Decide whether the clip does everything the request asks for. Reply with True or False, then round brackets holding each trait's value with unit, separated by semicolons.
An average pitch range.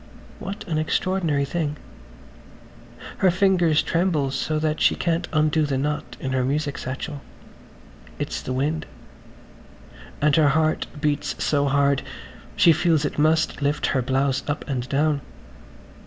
False (2.3 semitones)